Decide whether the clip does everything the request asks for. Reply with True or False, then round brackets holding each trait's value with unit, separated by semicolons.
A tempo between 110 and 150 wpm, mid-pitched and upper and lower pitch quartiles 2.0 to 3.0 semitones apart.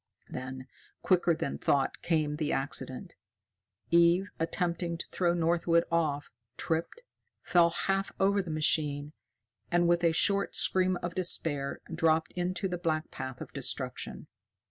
True (135 wpm; 170 Hz; 2.5 semitones)